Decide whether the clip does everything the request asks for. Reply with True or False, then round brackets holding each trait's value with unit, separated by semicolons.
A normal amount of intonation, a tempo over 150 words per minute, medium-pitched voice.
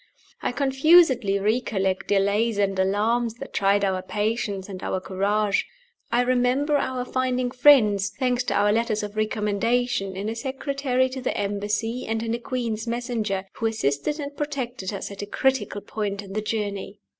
False (3.8 semitones; 165 wpm; 220 Hz)